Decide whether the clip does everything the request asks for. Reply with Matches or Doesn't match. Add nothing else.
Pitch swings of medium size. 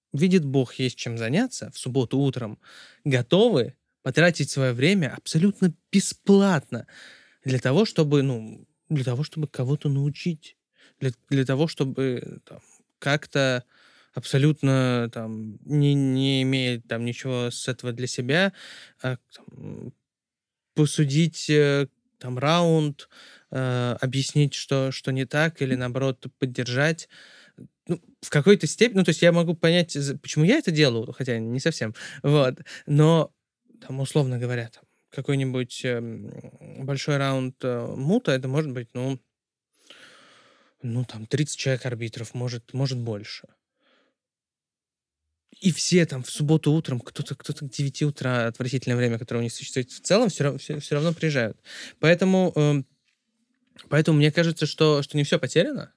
Matches